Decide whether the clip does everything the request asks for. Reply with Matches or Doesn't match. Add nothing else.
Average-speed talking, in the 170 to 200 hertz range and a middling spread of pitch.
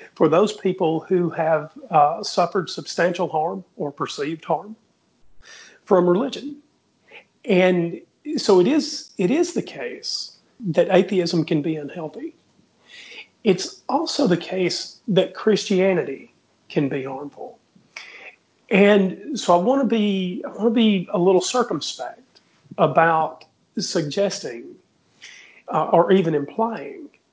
Doesn't match